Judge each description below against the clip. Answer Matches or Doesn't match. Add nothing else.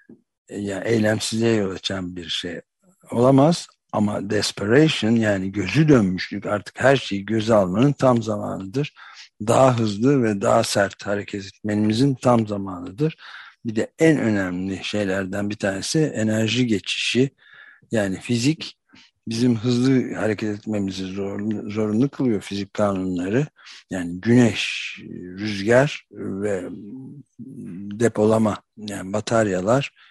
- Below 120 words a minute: Matches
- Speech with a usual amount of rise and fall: Matches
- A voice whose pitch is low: Matches